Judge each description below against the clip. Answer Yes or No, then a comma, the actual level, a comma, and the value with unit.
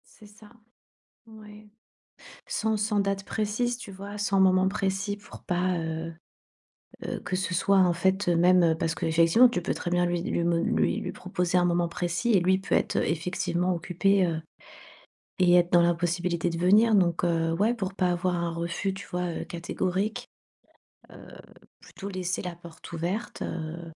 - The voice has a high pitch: No, medium, 180 Hz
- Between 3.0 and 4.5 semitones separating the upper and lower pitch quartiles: No, narrow, 2.4 semitones